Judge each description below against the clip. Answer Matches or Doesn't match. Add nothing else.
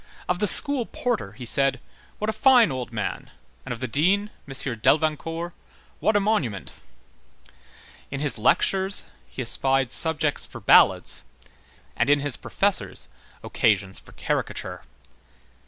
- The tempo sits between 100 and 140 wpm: Matches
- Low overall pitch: Doesn't match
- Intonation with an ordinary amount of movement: Doesn't match